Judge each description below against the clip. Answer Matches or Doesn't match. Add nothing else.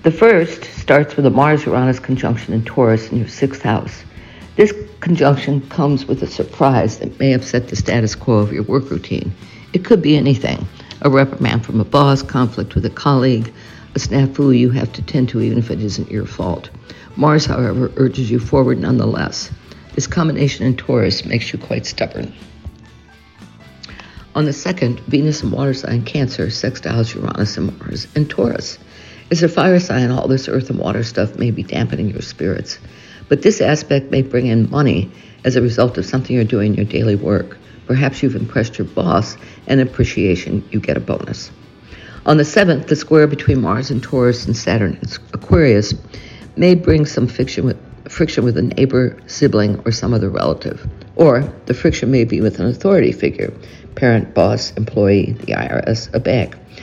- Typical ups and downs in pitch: Matches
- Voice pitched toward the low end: Matches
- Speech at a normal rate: Matches